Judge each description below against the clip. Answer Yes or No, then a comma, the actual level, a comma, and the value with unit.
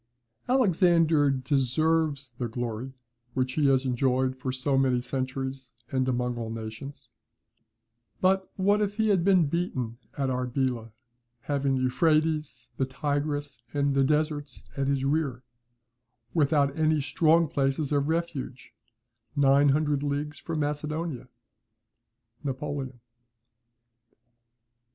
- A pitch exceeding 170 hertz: No, medium, 140 Hz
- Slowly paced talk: Yes, slow, 115 wpm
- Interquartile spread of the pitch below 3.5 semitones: Yes, average, 3.0 semitones